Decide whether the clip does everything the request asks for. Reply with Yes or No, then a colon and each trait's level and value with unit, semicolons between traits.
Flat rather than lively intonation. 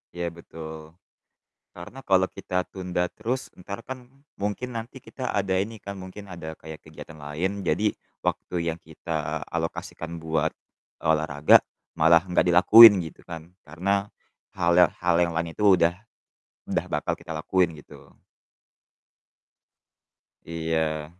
No: average, 3.2 semitones